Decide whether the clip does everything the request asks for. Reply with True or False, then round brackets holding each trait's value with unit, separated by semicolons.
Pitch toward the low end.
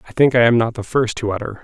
True (115 Hz)